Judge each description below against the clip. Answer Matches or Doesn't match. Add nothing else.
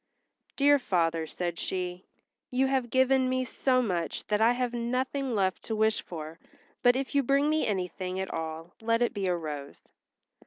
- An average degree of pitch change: Doesn't match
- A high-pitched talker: Matches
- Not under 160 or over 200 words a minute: Matches